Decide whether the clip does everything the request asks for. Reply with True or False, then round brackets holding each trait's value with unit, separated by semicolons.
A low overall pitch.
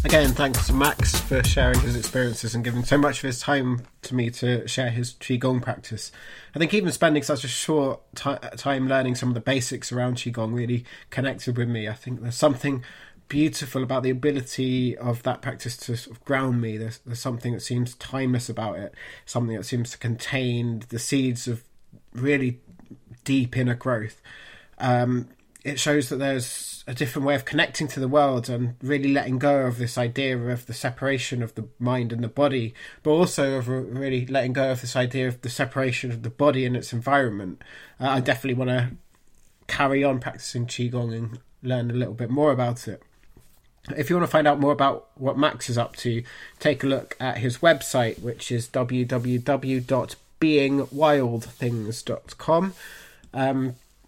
True (125 Hz)